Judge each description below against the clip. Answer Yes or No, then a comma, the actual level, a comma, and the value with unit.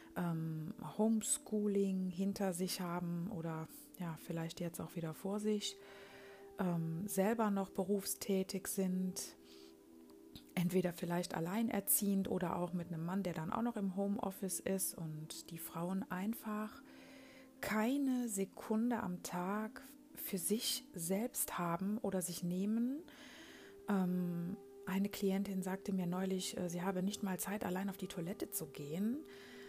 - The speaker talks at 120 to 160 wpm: Yes, average, 130 wpm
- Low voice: No, high, 195 Hz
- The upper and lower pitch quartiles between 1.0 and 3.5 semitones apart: Yes, average, 3.1 semitones